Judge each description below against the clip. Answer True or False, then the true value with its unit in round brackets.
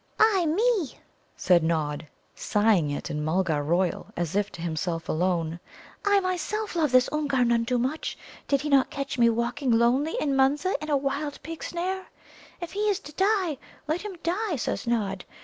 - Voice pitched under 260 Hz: False (270 Hz)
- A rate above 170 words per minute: True (180 wpm)